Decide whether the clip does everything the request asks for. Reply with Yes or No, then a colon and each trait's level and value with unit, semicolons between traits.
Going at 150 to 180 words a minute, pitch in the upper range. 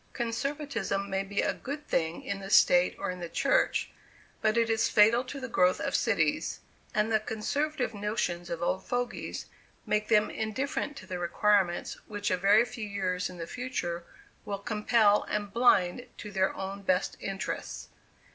Yes: average, 170 wpm; high, 210 Hz